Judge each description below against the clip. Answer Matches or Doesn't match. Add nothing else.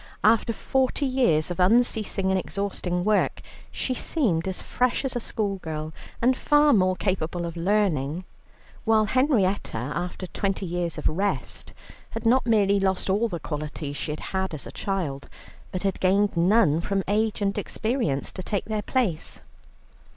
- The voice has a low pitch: Doesn't match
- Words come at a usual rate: Matches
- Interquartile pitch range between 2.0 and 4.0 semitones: Doesn't match